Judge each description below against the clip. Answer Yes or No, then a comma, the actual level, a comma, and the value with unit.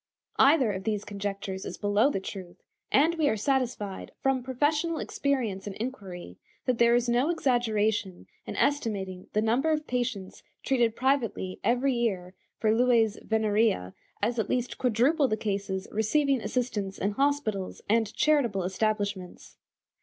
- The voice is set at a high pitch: Yes, high, 225 Hz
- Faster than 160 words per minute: No, average, 145 wpm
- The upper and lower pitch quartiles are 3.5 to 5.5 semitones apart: Yes, average, 4.5 semitones